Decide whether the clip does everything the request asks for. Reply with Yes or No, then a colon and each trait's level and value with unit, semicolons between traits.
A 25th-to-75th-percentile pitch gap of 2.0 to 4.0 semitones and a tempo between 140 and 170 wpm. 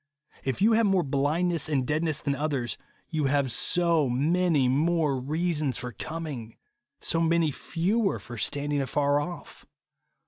Yes: average, 3.6 semitones; average, 145 wpm